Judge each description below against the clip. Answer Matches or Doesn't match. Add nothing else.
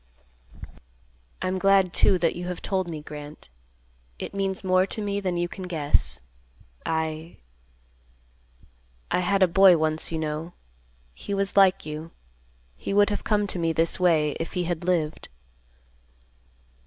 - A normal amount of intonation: Matches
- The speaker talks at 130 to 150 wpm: Matches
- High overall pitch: Doesn't match